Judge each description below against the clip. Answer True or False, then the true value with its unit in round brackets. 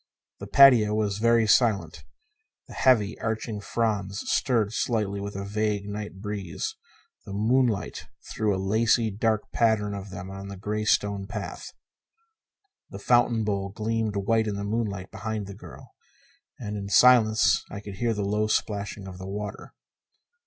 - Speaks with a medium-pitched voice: False (105 Hz)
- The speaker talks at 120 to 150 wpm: False (160 wpm)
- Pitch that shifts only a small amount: True (1.9 semitones)